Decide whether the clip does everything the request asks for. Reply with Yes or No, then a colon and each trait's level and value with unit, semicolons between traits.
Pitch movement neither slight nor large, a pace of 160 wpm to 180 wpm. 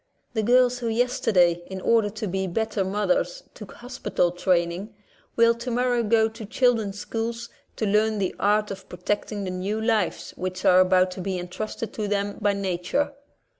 Yes: average, 3.6 semitones; average, 170 wpm